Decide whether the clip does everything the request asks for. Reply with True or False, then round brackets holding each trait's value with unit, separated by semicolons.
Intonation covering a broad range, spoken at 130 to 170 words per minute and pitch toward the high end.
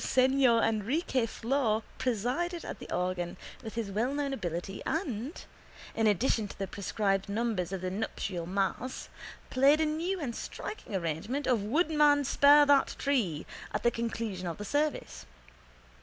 True (6.2 semitones; 145 wpm; 230 Hz)